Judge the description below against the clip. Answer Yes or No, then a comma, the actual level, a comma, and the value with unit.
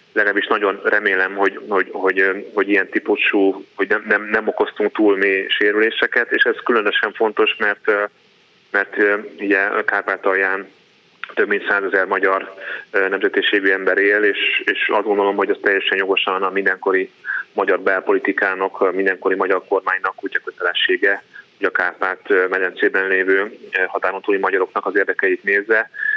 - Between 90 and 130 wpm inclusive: No, average, 145 wpm